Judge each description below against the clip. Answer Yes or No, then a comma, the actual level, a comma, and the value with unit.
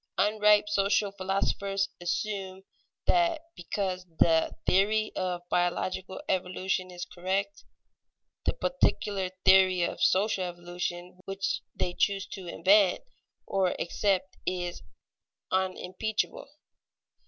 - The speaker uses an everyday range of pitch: No, narrow, 1.8 semitones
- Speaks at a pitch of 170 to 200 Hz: Yes, high, 190 Hz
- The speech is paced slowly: Yes, slow, 95 wpm